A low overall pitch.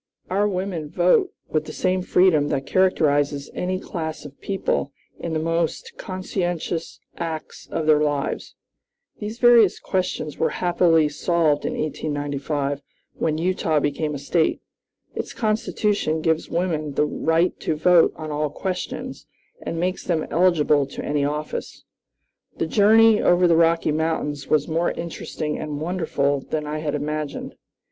No: medium, 160 Hz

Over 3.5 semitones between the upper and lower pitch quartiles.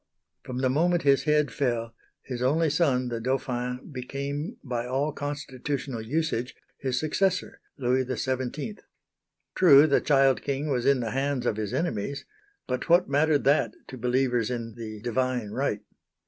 No: average, 2.8 semitones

